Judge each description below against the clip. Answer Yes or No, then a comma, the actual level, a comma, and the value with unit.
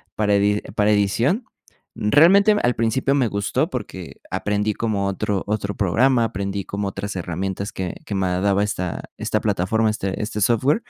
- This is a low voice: Yes, low, 105 Hz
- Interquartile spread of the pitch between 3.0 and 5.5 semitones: No, narrow, 2.5 semitones